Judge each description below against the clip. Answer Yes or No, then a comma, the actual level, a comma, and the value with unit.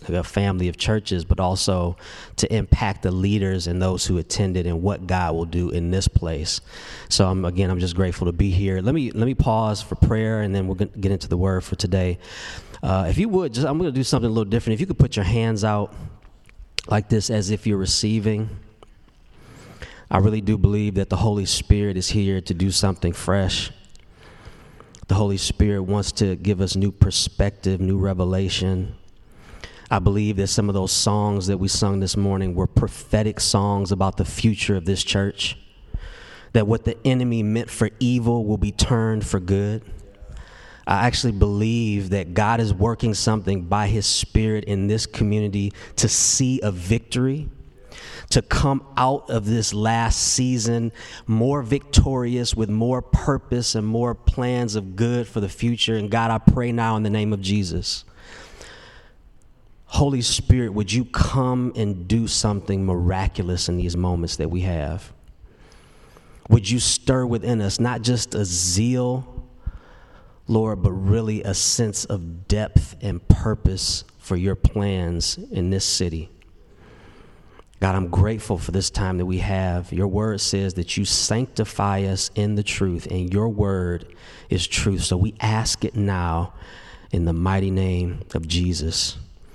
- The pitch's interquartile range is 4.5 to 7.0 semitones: No, average, 3.1 semitones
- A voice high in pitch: No, low, 100 Hz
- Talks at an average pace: Yes, average, 170 wpm